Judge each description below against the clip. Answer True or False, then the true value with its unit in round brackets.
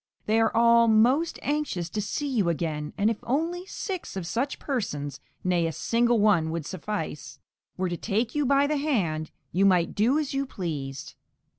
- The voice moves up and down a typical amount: False (8.2 semitones)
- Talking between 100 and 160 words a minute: False (180 wpm)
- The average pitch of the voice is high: True (215 Hz)